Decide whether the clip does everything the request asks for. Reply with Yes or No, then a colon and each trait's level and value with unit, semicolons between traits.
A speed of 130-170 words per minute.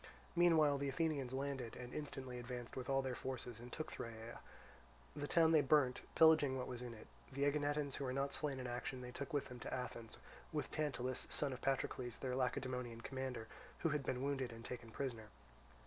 No: average, 195 wpm